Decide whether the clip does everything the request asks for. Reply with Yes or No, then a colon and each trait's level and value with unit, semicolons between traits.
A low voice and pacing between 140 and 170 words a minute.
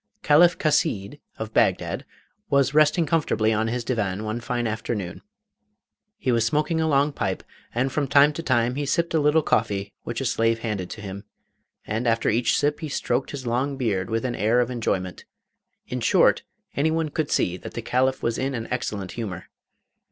No: low, 120 Hz; average, 185 wpm